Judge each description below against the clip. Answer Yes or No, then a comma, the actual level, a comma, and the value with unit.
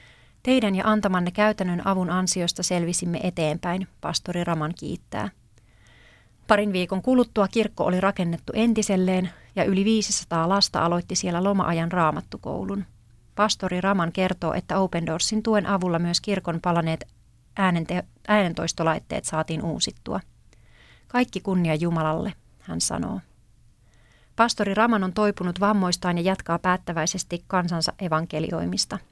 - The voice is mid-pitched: Yes, medium, 180 Hz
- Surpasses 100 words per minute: Yes, average, 115 wpm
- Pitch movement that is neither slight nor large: Yes, average, 3.6 semitones